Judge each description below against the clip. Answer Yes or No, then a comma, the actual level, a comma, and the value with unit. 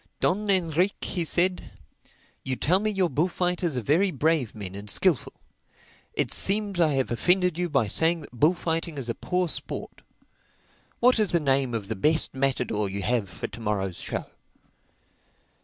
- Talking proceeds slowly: No, average, 165 wpm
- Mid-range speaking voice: Yes, medium, 160 Hz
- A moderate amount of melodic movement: No, wide, 6.9 semitones